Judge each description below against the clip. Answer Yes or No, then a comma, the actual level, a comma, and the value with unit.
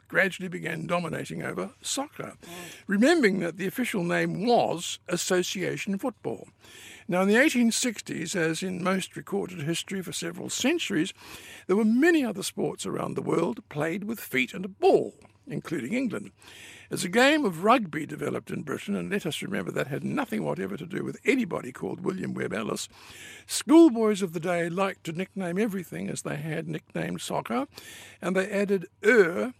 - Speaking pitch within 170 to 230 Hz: Yes, high, 190 Hz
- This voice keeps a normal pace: Yes, average, 165 wpm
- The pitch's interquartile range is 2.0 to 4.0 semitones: No, average, 4.8 semitones